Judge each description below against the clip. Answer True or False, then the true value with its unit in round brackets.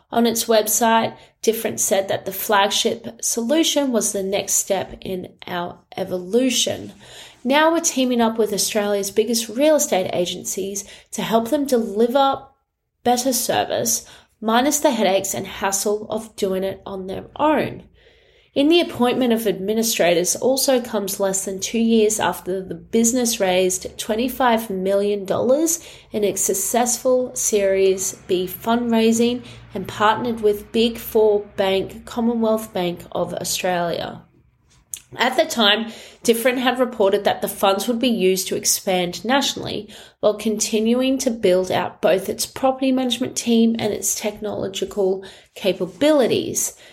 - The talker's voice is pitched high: True (215 Hz)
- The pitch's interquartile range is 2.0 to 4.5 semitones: True (3.9 semitones)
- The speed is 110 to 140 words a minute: True (135 wpm)